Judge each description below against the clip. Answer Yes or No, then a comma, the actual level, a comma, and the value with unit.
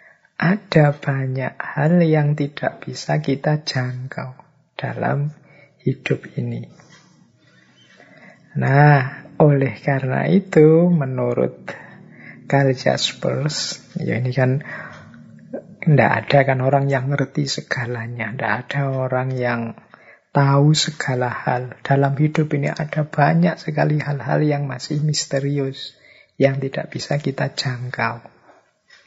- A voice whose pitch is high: No, medium, 140 Hz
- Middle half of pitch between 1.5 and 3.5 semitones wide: Yes, average, 2.8 semitones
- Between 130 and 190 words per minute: No, average, 105 wpm